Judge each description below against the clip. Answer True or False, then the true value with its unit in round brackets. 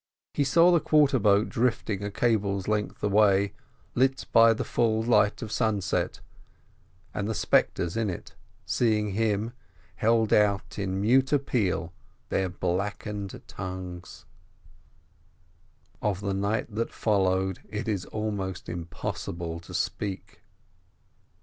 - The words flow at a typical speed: False (120 wpm)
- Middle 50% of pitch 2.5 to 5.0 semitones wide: True (2.9 semitones)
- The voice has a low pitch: True (105 Hz)